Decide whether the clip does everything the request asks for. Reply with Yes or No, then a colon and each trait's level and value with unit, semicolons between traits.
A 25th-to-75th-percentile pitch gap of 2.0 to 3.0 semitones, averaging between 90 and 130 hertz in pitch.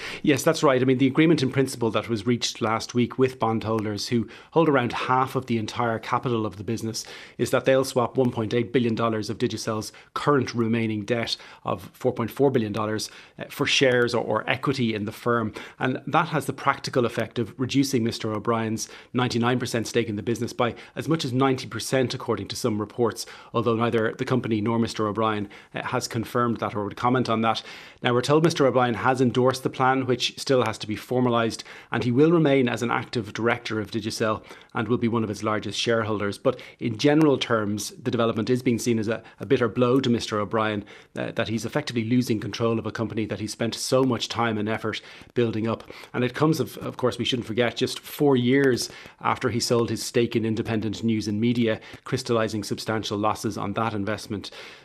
Yes: narrow, 2.5 semitones; low, 115 Hz